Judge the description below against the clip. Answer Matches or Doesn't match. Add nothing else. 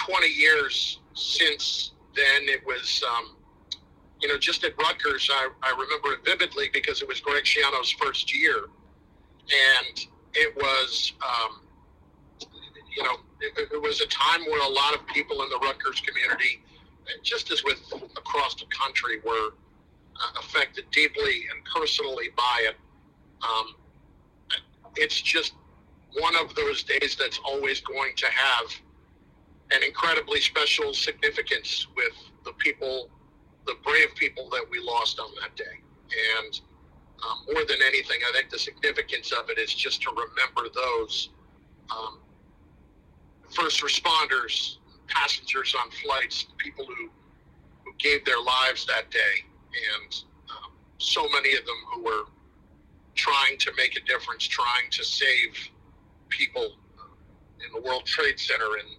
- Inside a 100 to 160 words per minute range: Matches